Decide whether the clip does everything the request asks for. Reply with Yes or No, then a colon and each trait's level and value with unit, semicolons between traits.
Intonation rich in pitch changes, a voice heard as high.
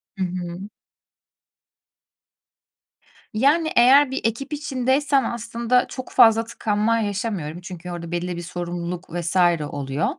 Yes: wide, 6.2 semitones; high, 210 Hz